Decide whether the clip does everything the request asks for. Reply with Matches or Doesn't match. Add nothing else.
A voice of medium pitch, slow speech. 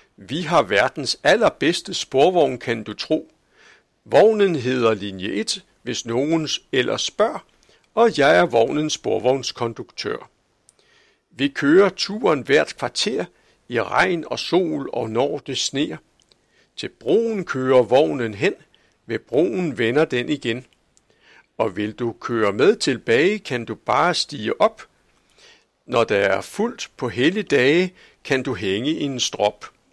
Doesn't match